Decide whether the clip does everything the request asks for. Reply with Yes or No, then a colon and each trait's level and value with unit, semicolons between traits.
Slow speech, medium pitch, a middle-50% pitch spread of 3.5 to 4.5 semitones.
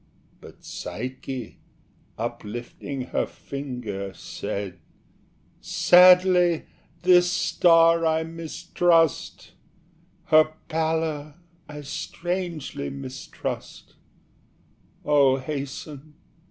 Yes: slow, 65 wpm; medium, 155 Hz; average, 3.8 semitones